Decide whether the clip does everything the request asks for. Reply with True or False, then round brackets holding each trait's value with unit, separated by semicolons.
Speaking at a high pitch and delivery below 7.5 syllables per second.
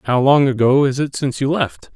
False (135 Hz; 5.6 syllables/s)